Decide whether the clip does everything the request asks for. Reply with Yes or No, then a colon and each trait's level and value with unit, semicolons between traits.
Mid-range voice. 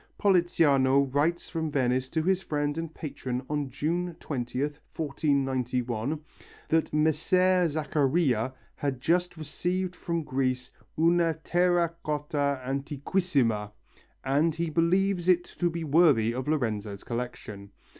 Yes: medium, 150 Hz